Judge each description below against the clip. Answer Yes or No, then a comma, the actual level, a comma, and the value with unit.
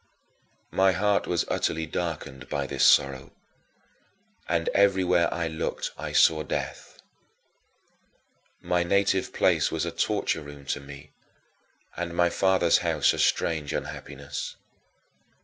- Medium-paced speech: No, slow, 125 wpm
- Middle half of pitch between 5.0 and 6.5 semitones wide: No, average, 3.7 semitones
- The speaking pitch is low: Yes, very low, 80 Hz